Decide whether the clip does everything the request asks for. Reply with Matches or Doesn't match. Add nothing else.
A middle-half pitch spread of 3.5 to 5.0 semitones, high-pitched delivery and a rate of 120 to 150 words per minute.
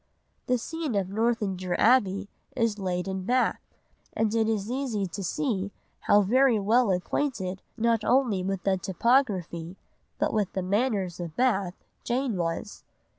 Matches